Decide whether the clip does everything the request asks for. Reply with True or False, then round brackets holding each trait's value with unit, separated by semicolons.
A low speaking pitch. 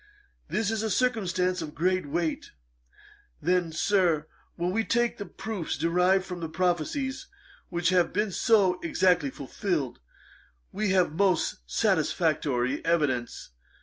False (180 Hz)